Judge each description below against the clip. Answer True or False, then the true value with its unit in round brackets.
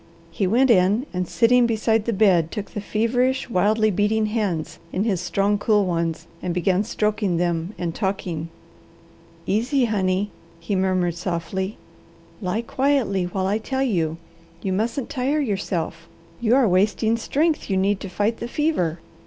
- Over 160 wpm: False (155 wpm)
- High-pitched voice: True (205 Hz)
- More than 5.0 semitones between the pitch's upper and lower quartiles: False (4.0 semitones)